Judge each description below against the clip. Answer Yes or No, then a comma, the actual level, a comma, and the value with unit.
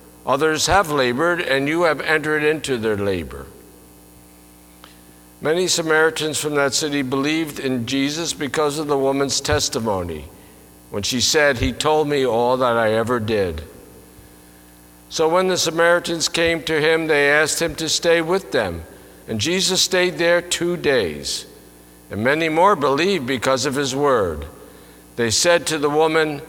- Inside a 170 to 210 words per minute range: No, average, 150 wpm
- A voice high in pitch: No, medium, 145 Hz